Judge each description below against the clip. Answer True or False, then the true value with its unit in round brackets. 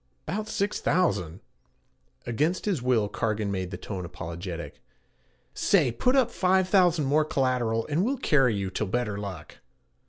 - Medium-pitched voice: False (125 Hz)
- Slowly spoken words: False (155 wpm)